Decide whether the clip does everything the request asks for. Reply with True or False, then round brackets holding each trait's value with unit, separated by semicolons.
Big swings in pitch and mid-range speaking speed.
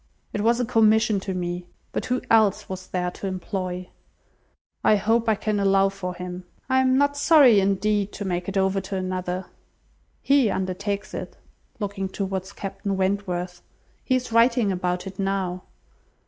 False (2.7 semitones; 160 wpm)